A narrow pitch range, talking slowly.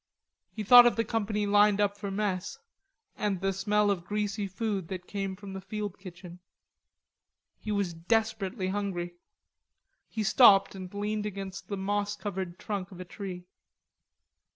No: narrow, 1.8 semitones; average, 150 wpm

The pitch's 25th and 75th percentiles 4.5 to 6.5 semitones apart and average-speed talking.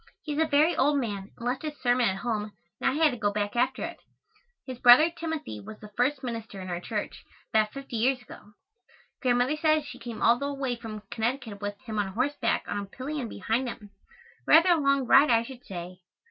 No: average, 4.8 semitones; fast, 215 wpm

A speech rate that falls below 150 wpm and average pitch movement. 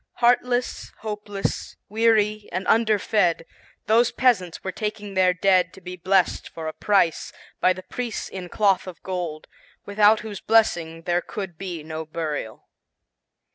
Yes: average, 140 wpm; average, 3.5 semitones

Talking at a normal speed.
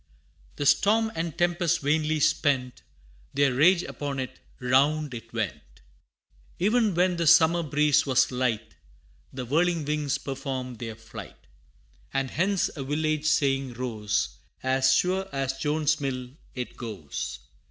No: slow, 130 wpm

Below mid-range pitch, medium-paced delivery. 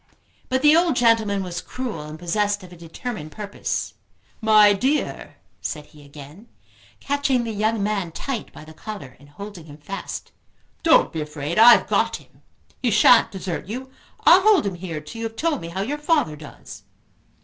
No: high, 205 Hz; average, 180 wpm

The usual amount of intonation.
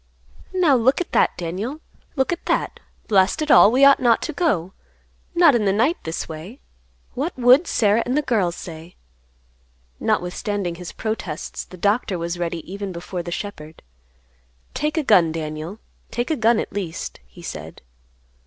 No: wide, 7.0 semitones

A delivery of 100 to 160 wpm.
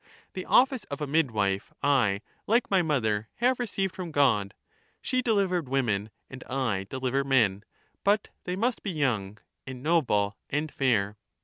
Yes: average, 150 wpm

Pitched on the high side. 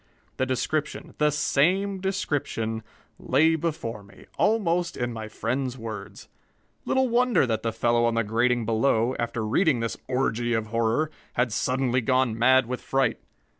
No: low, 125 Hz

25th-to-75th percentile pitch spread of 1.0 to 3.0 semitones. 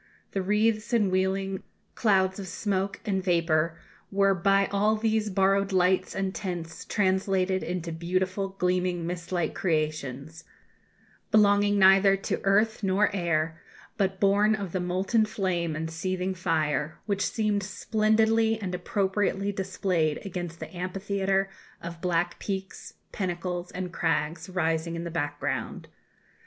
Yes: narrow, 2.6 semitones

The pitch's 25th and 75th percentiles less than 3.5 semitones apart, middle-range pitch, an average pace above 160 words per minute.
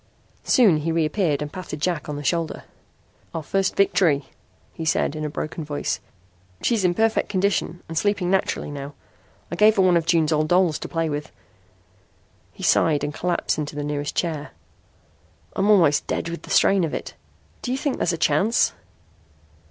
No: average, 4.1 semitones; medium, 165 Hz; average, 180 wpm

